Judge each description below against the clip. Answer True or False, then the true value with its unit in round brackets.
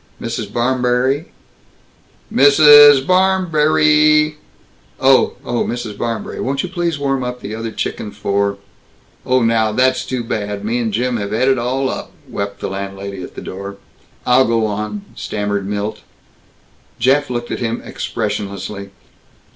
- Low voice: True (120 Hz)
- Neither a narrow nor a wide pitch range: True (4.7 semitones)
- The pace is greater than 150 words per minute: False (145 wpm)